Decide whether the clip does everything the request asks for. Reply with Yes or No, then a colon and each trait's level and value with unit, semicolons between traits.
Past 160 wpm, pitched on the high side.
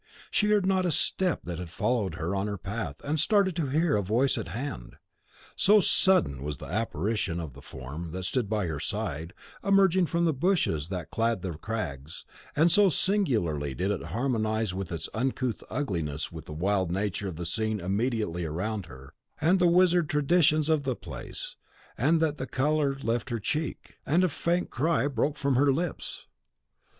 No: average, 180 wpm; low, 115 Hz